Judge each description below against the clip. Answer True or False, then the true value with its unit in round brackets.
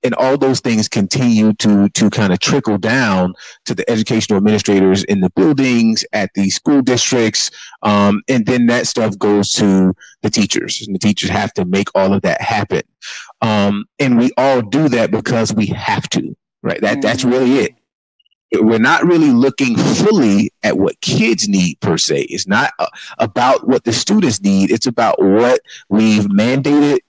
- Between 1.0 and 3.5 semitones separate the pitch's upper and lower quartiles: False (4.1 semitones)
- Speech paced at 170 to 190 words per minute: True (175 wpm)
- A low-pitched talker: True (110 Hz)